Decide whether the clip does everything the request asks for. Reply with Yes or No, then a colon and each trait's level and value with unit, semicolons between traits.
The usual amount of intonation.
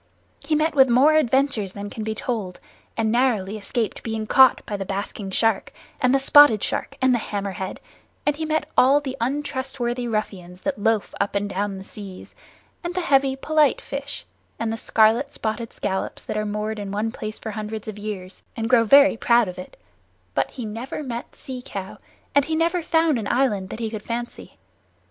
Yes: average, 4.6 semitones